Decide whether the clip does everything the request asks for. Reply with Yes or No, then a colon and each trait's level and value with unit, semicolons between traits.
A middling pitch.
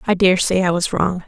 Yes: medium, 180 Hz